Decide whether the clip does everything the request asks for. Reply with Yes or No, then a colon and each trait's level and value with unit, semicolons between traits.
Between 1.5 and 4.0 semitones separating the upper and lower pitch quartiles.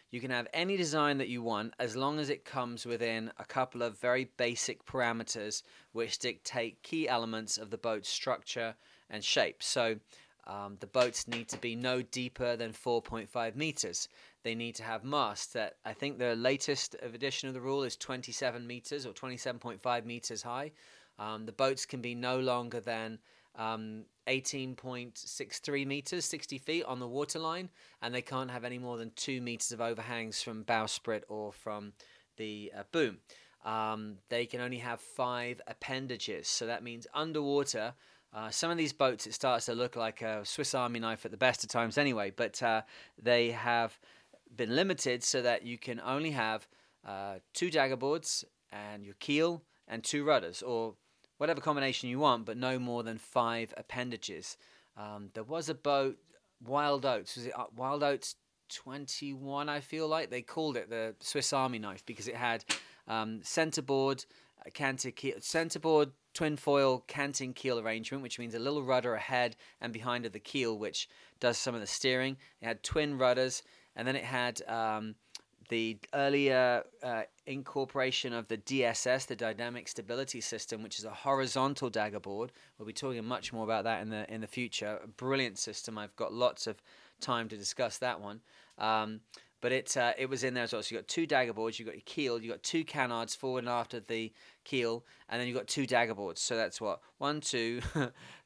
Yes: average, 3.0 semitones